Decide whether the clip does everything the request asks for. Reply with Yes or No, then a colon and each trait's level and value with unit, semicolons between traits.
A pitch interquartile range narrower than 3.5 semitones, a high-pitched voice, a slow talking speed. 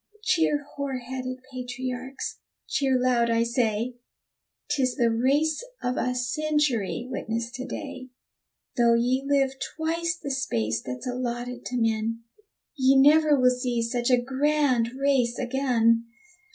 Yes: narrow, 2.5 semitones; very high, 255 Hz; slow, 130 wpm